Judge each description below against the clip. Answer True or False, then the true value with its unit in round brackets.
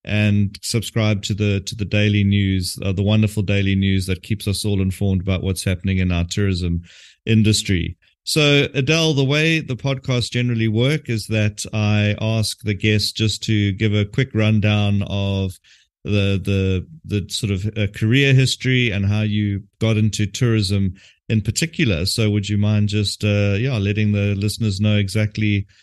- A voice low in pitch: True (105 Hz)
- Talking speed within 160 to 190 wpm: True (170 wpm)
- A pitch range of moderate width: False (1.8 semitones)